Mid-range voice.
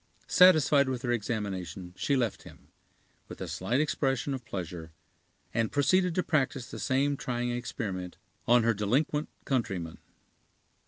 No: low, 120 Hz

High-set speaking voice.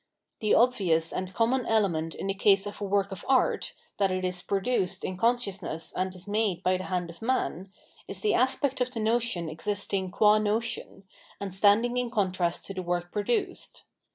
Yes: high, 200 Hz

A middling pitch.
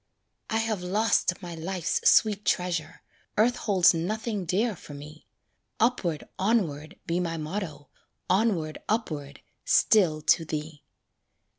Yes: medium, 180 Hz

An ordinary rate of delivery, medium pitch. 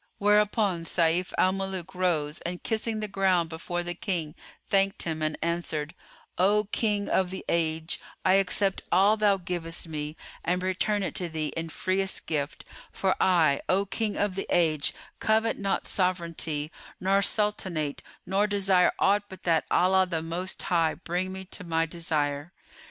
Yes: average, 160 wpm; medium, 180 Hz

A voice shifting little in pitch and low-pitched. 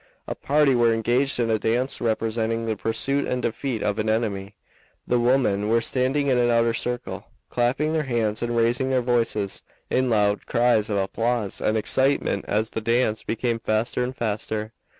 Yes: narrow, 2.3 semitones; low, 115 Hz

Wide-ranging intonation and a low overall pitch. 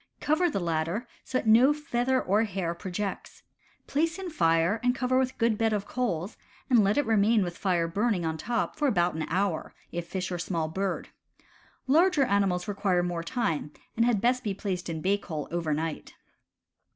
No: wide, 6.0 semitones; high, 200 Hz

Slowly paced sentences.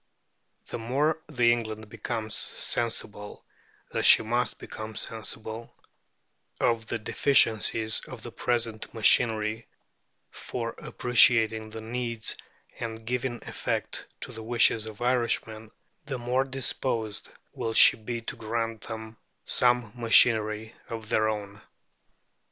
Yes: slow, 115 wpm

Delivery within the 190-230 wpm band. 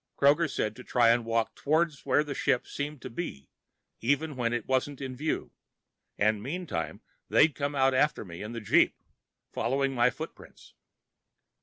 No: average, 165 wpm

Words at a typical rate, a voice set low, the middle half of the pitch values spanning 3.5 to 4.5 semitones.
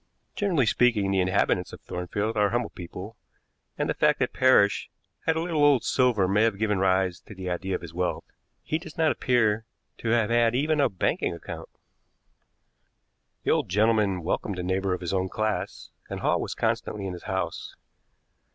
Yes: average, 185 wpm; low, 105 Hz; average, 4.2 semitones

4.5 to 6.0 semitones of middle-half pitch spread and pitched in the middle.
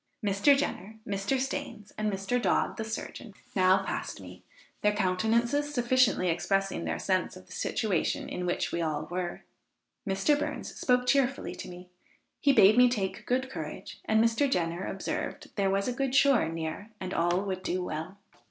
No: average, 5.1 semitones; high, 200 Hz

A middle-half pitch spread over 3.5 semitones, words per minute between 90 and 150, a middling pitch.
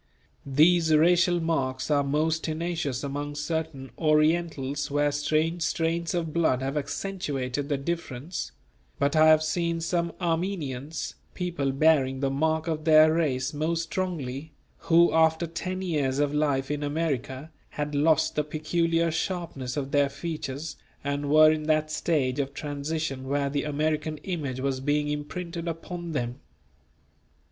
No: average, 2.7 semitones; average, 140 wpm; medium, 155 Hz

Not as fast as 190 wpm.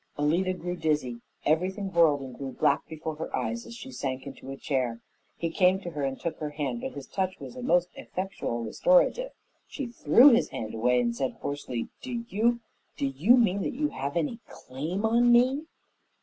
No: average, 195 wpm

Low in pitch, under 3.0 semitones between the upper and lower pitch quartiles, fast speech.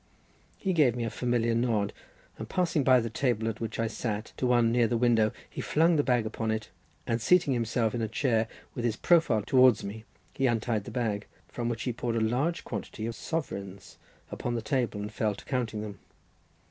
Yes: low, 115 Hz; narrow, 2.4 semitones; fast, 210 wpm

